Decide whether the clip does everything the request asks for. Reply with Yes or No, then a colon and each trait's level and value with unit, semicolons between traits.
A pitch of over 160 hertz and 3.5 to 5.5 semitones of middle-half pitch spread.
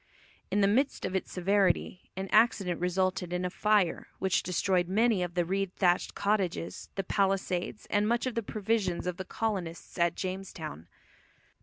No: high, 190 Hz; narrow, 2.5 semitones